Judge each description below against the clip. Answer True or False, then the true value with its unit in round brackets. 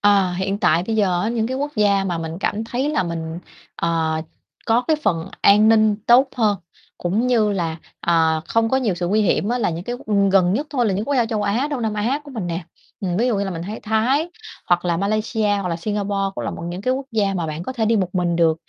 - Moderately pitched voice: False (205 Hz)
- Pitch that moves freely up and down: False (4.4 semitones)